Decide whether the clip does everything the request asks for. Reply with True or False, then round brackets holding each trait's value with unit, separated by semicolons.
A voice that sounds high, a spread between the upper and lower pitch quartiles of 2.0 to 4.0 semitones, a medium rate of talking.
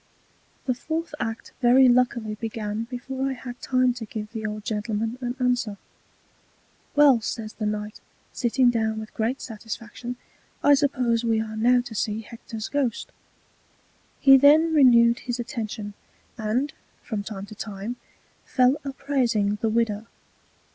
True (235 Hz; 2.6 semitones; 145 wpm)